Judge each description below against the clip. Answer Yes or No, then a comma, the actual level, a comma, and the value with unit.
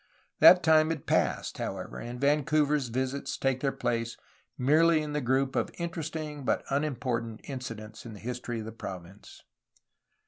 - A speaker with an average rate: Yes, average, 150 wpm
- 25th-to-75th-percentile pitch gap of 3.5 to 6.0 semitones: Yes, average, 4.3 semitones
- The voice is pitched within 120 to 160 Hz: Yes, low, 135 Hz